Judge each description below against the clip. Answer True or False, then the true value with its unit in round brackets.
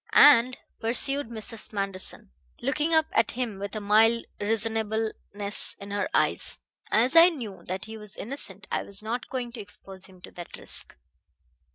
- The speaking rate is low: False (165 wpm)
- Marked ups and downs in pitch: False (3.3 semitones)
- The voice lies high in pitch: True (220 Hz)